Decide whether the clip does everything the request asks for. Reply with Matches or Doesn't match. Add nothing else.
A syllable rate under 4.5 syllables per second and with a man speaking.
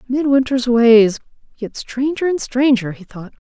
Doesn't match